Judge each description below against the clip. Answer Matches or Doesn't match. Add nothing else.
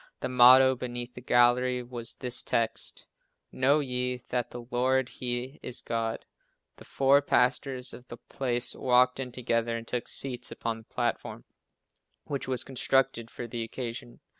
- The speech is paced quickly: Doesn't match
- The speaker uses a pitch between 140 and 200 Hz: Doesn't match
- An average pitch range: Doesn't match